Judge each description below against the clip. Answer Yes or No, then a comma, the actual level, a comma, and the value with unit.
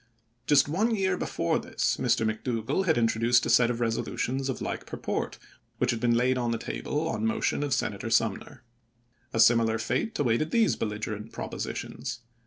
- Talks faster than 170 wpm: Yes, average, 180 wpm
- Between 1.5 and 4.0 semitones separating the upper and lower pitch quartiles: No, average, 4.5 semitones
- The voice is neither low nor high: No, low, 120 Hz